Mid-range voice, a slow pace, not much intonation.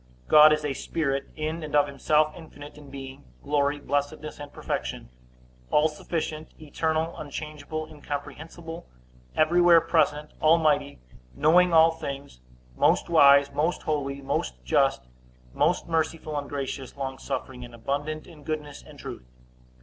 Yes: medium, 150 Hz; slow, 130 wpm; narrow, 2.0 semitones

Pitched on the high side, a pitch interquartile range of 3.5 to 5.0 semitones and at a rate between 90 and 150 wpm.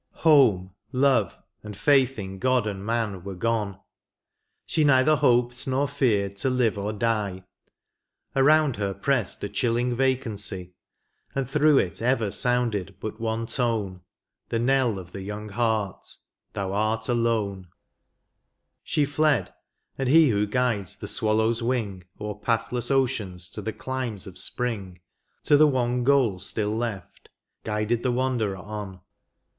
No: low, 115 Hz; average, 4.2 semitones; average, 145 wpm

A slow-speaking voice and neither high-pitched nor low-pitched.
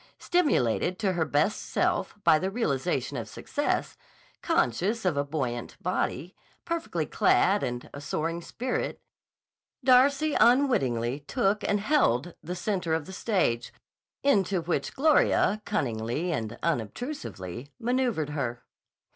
Yes: slow, 120 wpm; medium, 180 Hz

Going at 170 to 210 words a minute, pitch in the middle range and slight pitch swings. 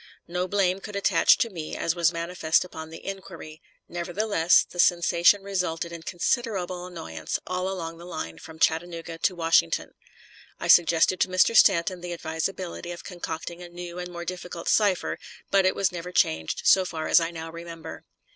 Yes: average, 175 wpm; medium, 175 Hz; narrow, 1.8 semitones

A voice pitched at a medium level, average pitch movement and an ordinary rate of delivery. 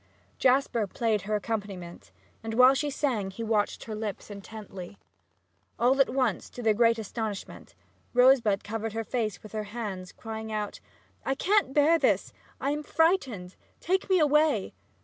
No: high, 225 Hz; average, 4.3 semitones; average, 160 wpm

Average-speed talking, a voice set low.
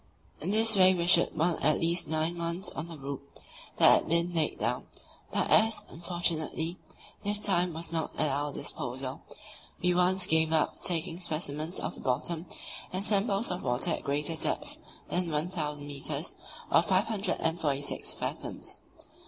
No: average, 155 wpm; medium, 165 Hz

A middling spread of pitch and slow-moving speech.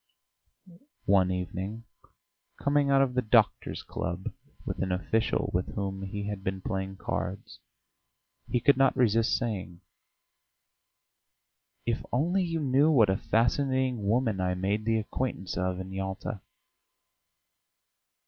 Yes: average, 5.0 semitones; slow, 125 wpm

